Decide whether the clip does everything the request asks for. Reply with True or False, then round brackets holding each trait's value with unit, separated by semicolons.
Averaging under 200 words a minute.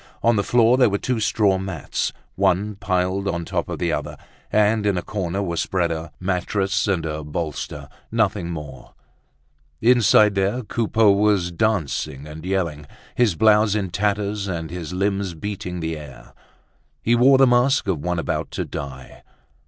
True (165 wpm)